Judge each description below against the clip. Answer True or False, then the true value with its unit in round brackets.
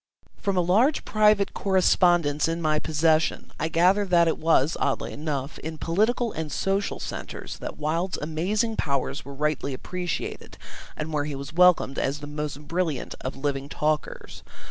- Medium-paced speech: True (160 wpm)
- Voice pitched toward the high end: False (160 Hz)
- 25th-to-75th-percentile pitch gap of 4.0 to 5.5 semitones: False (3.6 semitones)